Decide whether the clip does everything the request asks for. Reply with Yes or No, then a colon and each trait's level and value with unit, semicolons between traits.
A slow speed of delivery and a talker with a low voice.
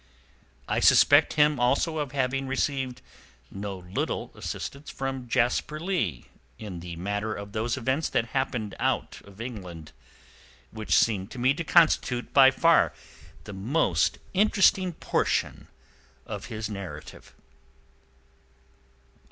Yes: slow, 120 wpm; low, 125 Hz